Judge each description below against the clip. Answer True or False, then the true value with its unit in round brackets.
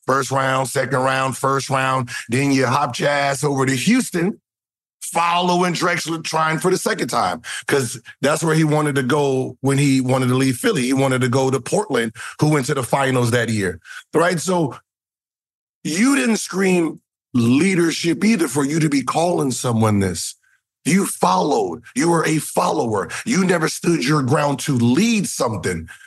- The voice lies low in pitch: False (145 Hz)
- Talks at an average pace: True (170 wpm)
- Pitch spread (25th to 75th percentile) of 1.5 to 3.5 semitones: False (4.3 semitones)